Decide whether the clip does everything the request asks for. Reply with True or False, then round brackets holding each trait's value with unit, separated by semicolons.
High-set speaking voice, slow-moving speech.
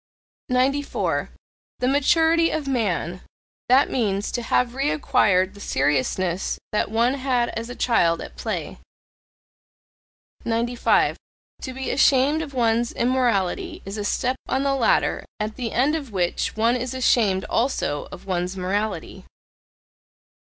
True (240 Hz; 130 wpm)